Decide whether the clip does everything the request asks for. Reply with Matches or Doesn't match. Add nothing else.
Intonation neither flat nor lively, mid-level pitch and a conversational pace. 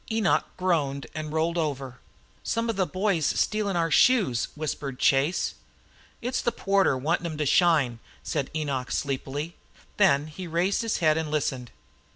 Matches